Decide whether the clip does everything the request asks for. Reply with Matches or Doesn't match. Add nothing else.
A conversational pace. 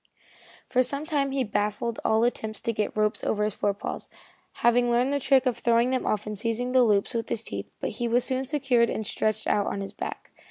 Doesn't match